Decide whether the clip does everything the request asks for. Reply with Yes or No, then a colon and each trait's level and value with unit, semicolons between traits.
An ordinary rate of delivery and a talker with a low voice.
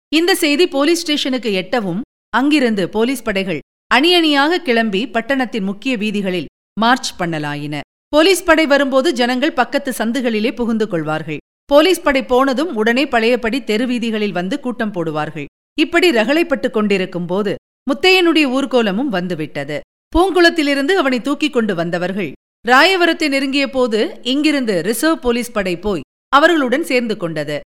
No: average, 120 wpm; very high, 250 Hz